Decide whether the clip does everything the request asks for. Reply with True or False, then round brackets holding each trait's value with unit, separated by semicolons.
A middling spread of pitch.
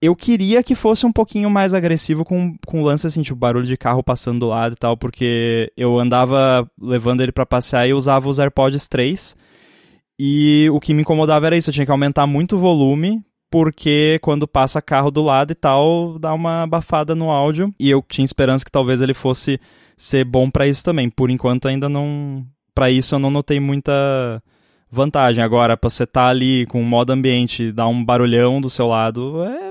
True (3.7 semitones)